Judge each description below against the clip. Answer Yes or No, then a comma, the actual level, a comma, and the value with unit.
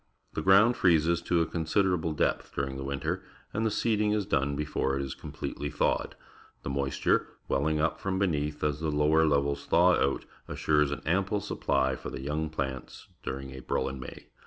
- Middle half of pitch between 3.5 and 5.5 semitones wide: Yes, average, 4.0 semitones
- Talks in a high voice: No, very low, 75 Hz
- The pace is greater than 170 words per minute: Yes, average, 185 wpm